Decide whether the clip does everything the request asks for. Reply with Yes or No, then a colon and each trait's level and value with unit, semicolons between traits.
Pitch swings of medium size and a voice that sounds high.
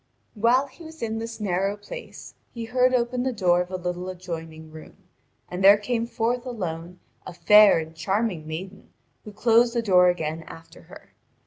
Yes: average, 4.8 semitones; high, 200 Hz